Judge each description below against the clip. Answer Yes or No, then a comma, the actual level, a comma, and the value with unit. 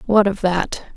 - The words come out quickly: No, average, 190 wpm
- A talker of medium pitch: No, high, 195 Hz